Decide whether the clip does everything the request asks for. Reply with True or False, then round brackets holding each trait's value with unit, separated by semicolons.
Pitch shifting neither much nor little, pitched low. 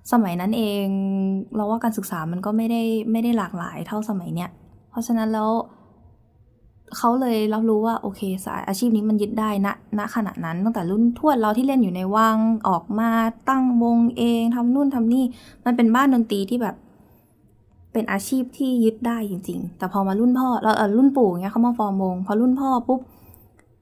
False (3.3 semitones; 220 Hz)